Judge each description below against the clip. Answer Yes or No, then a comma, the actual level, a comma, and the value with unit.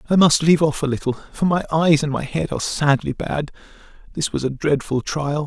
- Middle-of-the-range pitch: Yes, medium, 150 Hz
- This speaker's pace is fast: Yes, fast, 210 wpm